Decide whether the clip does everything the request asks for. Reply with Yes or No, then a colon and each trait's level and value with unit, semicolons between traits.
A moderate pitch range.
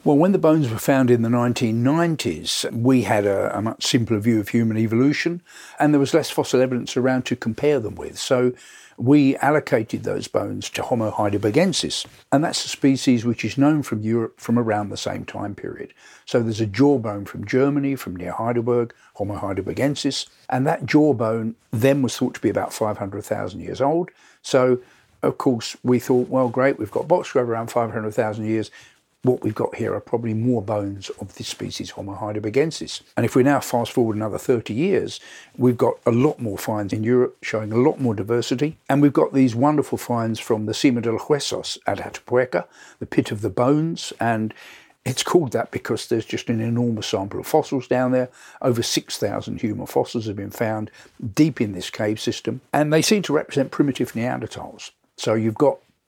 Yes: average, 3.5 semitones